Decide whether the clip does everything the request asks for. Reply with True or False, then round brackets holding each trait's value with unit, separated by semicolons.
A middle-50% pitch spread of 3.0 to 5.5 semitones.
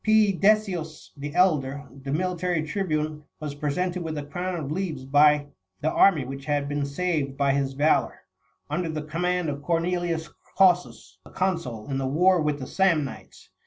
True (3.9 semitones)